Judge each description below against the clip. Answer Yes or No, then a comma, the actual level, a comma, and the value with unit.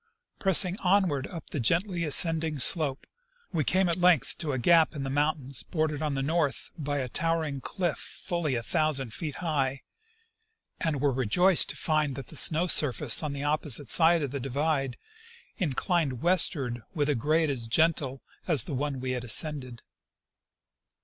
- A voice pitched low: No, medium, 150 Hz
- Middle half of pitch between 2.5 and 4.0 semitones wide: Yes, average, 3.6 semitones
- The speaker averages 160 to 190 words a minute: Yes, average, 170 wpm